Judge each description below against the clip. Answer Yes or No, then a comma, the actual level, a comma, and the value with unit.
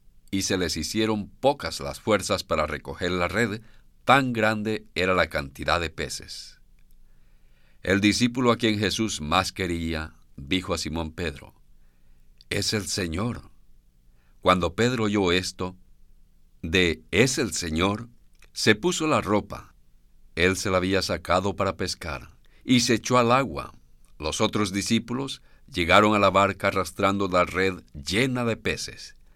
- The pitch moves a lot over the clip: Yes, wide, 7.2 semitones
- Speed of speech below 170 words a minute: Yes, average, 140 wpm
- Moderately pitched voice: No, very low, 90 Hz